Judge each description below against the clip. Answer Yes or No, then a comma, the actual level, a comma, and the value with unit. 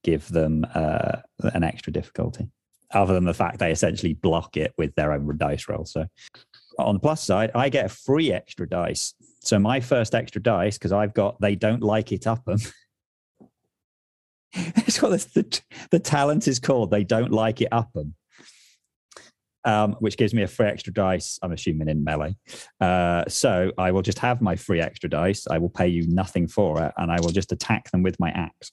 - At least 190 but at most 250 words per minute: Yes, average, 200 wpm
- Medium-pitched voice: No, low, 100 Hz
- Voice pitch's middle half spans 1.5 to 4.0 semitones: No, average, 4.5 semitones